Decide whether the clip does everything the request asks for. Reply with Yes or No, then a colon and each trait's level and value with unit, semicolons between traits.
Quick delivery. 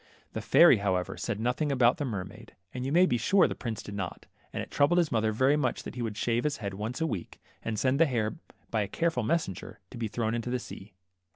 Yes: fast, 255 wpm